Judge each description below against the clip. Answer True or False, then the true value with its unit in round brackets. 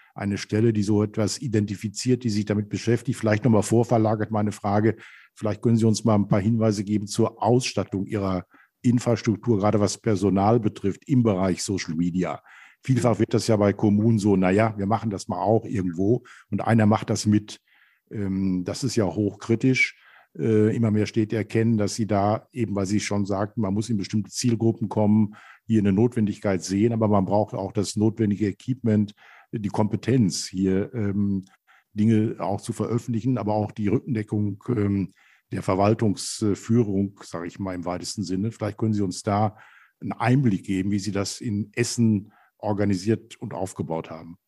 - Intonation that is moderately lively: False (2.1 semitones)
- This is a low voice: True (105 Hz)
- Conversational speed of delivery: True (170 wpm)